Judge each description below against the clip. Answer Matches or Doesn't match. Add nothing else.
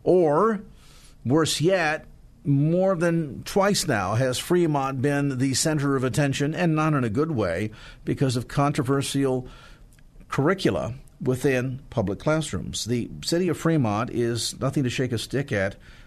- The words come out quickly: Doesn't match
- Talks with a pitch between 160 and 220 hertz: Doesn't match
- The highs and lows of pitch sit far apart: Doesn't match